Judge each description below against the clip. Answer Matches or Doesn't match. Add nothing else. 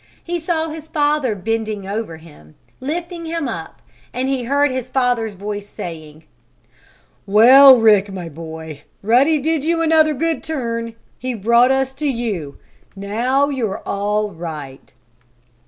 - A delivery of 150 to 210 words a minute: Doesn't match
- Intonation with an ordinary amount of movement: Doesn't match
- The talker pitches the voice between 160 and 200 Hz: Doesn't match